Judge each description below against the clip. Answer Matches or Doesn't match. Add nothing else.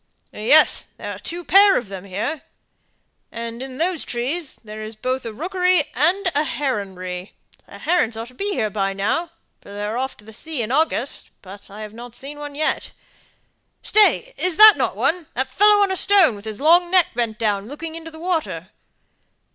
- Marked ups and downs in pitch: Matches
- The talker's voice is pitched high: Matches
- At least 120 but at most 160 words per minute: Doesn't match